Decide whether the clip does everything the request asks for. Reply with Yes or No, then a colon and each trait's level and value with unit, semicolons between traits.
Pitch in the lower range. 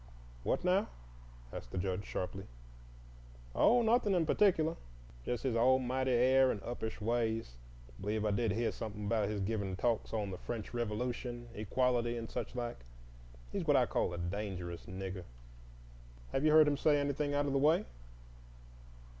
Yes: low, 115 Hz